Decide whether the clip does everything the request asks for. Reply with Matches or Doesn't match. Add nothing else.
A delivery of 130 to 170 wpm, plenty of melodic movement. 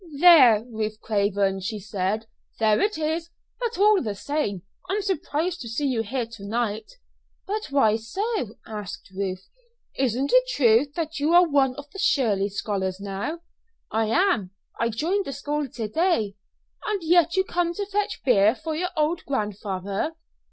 Matches